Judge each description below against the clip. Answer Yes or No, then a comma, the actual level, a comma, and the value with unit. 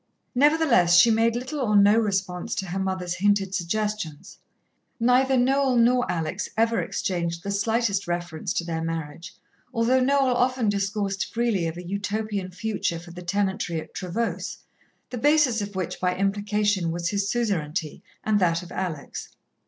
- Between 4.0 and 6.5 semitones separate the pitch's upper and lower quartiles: Yes, average, 4.6 semitones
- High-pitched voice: Yes, high, 200 Hz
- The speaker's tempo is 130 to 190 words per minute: Yes, average, 155 wpm